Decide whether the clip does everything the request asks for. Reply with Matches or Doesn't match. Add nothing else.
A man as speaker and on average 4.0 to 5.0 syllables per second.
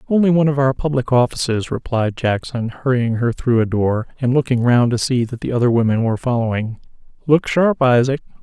Doesn't match